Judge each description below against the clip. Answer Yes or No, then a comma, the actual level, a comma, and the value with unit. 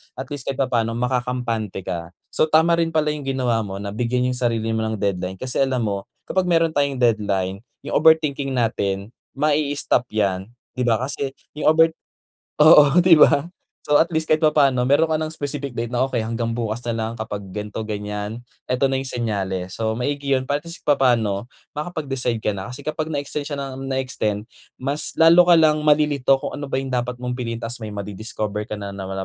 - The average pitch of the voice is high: No, low, 125 Hz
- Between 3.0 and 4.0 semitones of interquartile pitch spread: No, average, 4.8 semitones